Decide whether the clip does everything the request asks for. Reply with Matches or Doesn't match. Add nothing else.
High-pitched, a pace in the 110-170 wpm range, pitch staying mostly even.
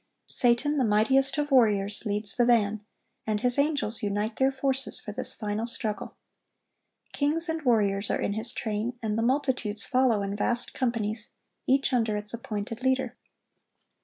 Doesn't match